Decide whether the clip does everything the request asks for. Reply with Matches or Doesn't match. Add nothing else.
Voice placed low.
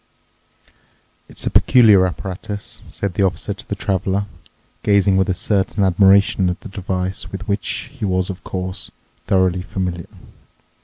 Matches